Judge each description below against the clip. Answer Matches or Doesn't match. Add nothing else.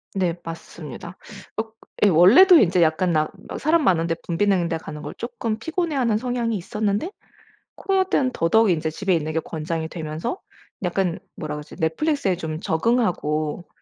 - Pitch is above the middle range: Doesn't match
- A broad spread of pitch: Matches